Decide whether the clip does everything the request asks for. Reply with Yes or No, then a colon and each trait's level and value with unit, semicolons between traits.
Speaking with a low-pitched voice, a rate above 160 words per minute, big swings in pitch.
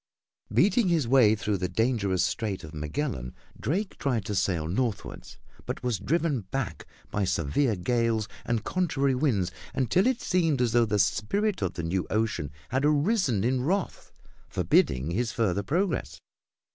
No: low, 115 Hz; average, 155 wpm; wide, 7.0 semitones